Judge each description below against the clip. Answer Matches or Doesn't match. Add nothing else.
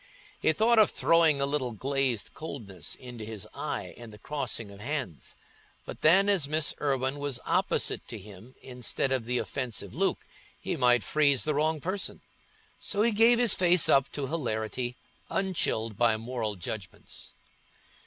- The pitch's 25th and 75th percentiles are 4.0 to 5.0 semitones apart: Doesn't match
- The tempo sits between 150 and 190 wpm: Matches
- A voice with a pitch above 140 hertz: Doesn't match